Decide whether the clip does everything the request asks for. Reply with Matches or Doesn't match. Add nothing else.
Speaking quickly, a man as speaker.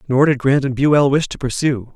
Matches